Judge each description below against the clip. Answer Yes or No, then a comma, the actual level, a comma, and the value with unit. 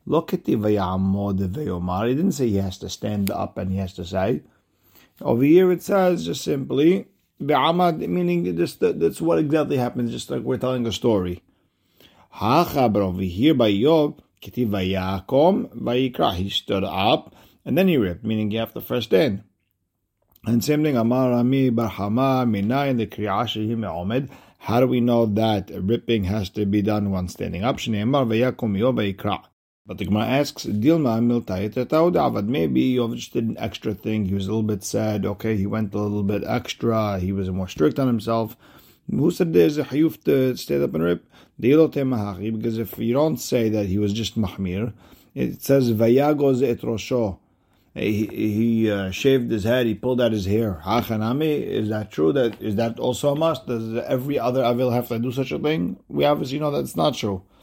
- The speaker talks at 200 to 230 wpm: No, average, 155 wpm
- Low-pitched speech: Yes, low, 110 Hz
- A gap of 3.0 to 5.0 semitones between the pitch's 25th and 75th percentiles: Yes, average, 4.3 semitones